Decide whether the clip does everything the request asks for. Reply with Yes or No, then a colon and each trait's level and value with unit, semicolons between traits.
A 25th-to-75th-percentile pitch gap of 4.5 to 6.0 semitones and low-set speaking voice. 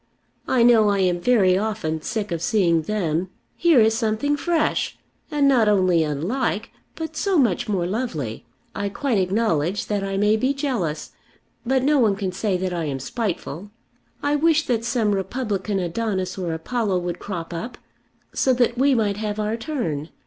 No: average, 5.2 semitones; high, 210 Hz